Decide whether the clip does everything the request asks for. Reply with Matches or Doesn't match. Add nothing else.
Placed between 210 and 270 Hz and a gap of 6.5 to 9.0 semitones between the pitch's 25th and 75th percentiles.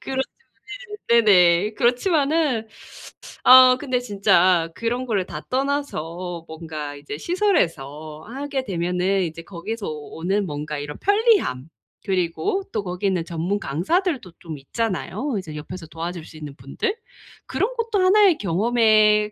Doesn't match